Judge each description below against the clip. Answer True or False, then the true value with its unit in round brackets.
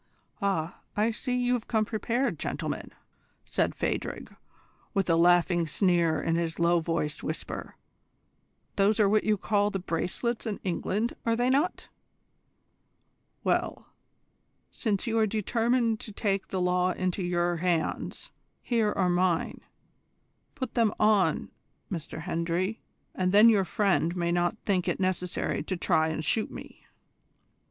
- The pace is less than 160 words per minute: True (145 wpm)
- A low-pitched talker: False (190 Hz)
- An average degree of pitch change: True (4.0 semitones)